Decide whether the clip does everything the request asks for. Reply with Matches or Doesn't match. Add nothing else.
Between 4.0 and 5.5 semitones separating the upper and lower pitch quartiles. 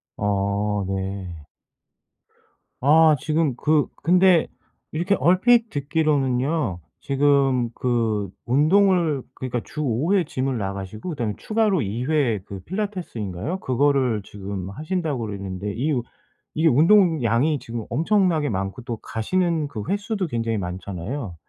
Doesn't match